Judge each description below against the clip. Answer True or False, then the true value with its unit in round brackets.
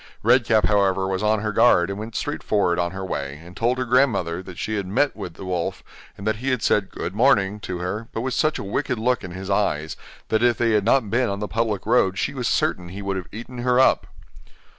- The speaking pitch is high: False (105 Hz)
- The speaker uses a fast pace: True (250 wpm)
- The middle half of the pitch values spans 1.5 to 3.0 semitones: False (4.0 semitones)